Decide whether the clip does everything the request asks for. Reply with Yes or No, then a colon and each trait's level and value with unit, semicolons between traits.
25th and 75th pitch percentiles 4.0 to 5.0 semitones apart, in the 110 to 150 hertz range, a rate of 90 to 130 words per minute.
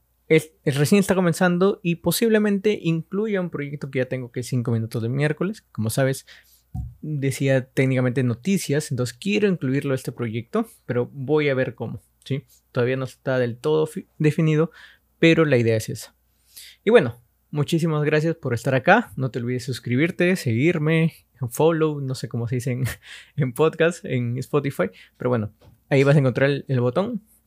No: average, 4.6 semitones; medium, 140 Hz; average, 175 wpm